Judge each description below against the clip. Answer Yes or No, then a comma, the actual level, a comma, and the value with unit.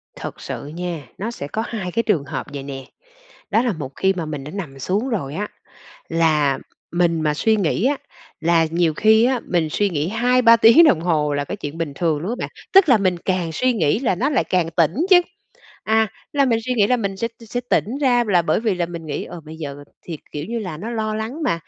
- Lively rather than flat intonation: Yes, wide, 6.2 semitones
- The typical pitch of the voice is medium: Yes, medium, 180 Hz